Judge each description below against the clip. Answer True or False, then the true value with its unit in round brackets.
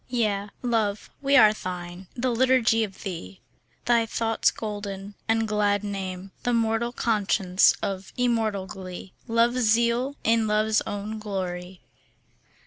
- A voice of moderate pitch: False (215 Hz)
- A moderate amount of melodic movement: True (3.0 semitones)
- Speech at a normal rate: False (130 wpm)